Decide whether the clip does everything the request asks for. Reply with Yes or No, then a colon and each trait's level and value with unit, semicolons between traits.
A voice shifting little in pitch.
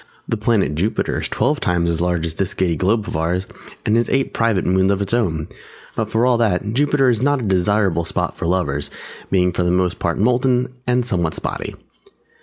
No: average, 5.1 semitones